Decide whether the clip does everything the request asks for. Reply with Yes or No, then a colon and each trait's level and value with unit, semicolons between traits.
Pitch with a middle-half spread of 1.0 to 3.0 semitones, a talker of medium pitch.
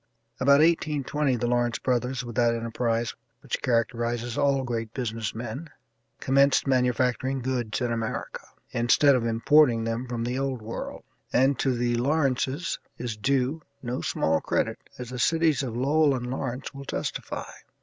No: average, 2.7 semitones; low, 125 Hz